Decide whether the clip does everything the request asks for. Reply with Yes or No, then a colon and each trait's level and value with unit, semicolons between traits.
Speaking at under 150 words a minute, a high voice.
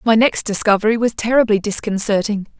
Yes: average, 140 wpm; high, 215 Hz